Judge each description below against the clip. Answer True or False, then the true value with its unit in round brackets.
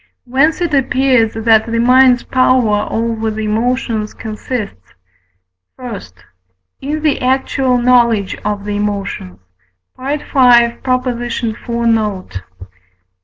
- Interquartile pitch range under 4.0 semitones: True (2.9 semitones)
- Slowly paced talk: True (100 wpm)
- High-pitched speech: True (235 Hz)